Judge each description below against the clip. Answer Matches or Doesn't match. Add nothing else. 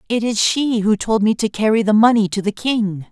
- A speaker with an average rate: Doesn't match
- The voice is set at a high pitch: Matches